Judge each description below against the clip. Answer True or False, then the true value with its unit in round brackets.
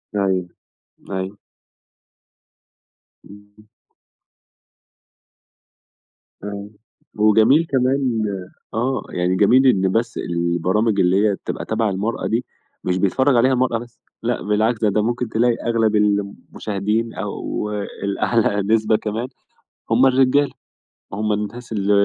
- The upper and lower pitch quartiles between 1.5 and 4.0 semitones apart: True (2.9 semitones)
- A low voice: True (110 Hz)